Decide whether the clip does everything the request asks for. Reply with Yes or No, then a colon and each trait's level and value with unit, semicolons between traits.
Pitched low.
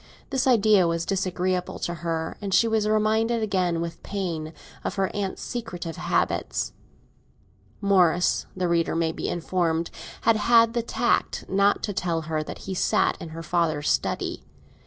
No: medium, 185 Hz